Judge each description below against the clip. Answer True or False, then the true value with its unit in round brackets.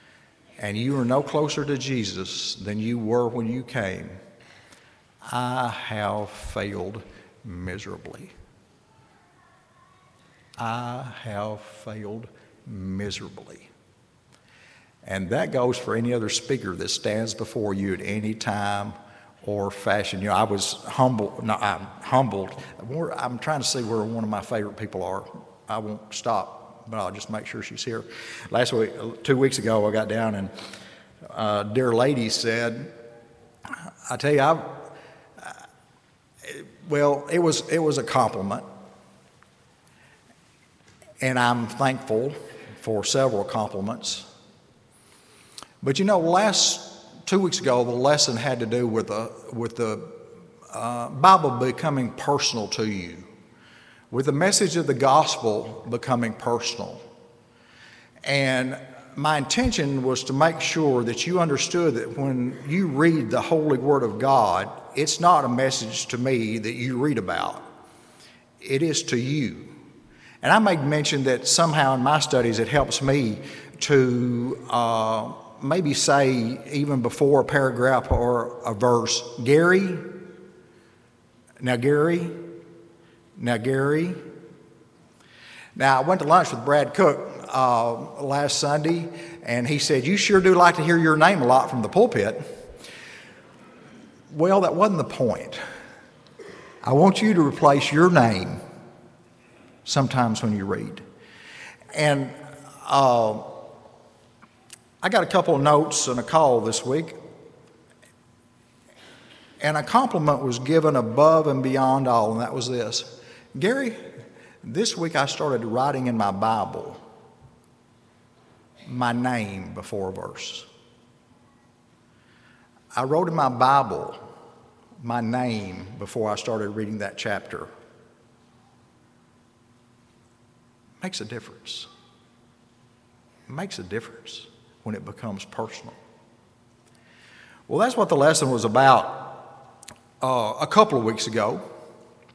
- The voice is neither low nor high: False (125 Hz)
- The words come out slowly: True (130 wpm)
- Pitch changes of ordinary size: True (4.5 semitones)